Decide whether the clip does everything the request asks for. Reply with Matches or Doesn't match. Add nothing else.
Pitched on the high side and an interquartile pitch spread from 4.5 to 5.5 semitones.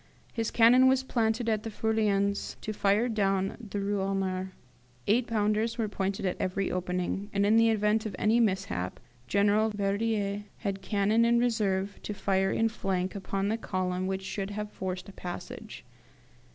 Doesn't match